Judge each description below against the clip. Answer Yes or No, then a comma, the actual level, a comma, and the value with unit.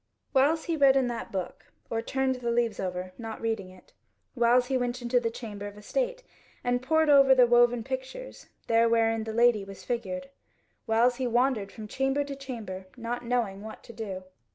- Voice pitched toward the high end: Yes, high, 240 Hz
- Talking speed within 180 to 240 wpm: Yes, average, 190 wpm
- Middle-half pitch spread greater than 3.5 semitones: No, average, 3.0 semitones